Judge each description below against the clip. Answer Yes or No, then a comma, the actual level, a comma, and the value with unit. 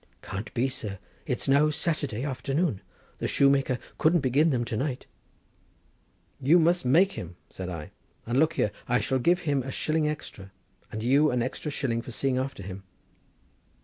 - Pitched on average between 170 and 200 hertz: No, low, 135 Hz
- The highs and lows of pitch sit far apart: No, average, 4.6 semitones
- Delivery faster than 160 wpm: Yes, average, 180 wpm